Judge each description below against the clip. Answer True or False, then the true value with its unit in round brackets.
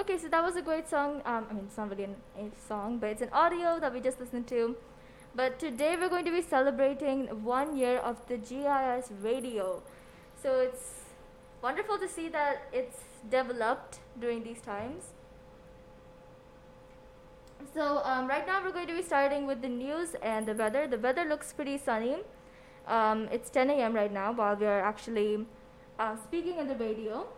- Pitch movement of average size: True (4.7 semitones)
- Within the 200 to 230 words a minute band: False (180 wpm)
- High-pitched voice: True (255 Hz)